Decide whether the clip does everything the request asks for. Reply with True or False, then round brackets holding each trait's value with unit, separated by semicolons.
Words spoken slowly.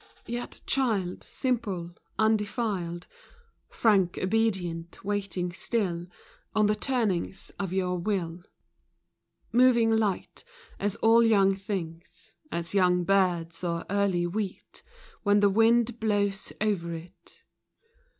True (105 wpm)